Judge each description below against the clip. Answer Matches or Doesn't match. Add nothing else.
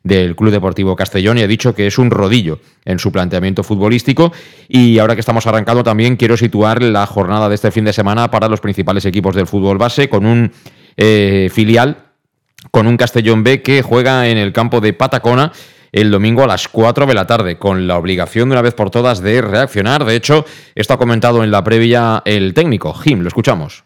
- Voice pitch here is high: Doesn't match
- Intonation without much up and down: Doesn't match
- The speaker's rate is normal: Doesn't match